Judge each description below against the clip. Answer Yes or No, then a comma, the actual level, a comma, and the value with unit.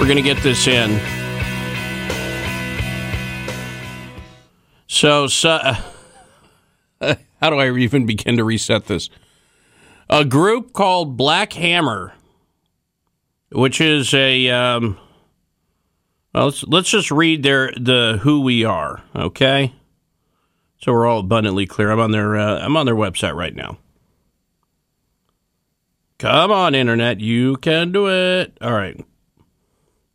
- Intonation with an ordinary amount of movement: No, wide, 8.3 semitones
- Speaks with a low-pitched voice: Yes, low, 115 Hz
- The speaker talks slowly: Yes, slow, 120 wpm